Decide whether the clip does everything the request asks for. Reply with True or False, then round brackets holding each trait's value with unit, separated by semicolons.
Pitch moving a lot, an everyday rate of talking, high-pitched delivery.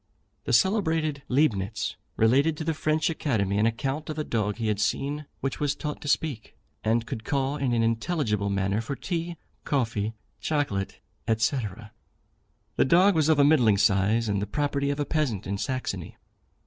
False (5.7 semitones; 175 wpm; 135 Hz)